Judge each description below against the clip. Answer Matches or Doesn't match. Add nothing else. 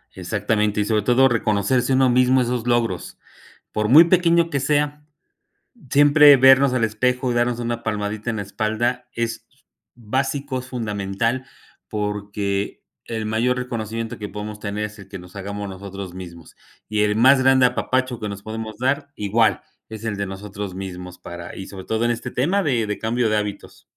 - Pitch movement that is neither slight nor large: Matches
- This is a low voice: Matches